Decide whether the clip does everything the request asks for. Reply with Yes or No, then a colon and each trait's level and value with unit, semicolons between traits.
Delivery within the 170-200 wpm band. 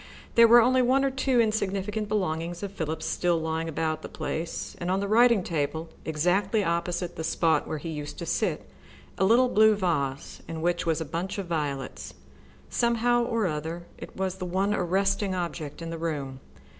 Yes: average, 180 wpm